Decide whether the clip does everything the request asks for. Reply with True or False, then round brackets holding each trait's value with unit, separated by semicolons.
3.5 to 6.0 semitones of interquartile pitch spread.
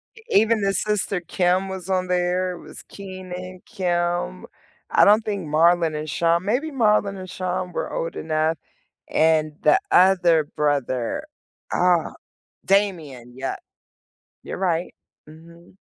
False (2.9 semitones)